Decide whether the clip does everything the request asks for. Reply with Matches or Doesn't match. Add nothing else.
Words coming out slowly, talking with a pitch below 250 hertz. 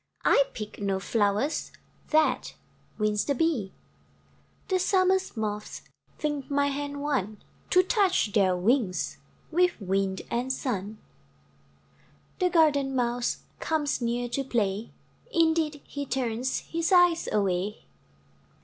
Doesn't match